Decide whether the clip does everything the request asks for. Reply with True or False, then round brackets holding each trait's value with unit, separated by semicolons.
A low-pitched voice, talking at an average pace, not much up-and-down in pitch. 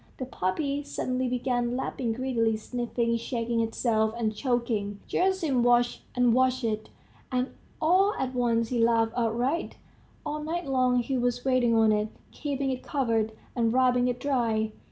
False (245 Hz; 155 wpm; 2.1 semitones)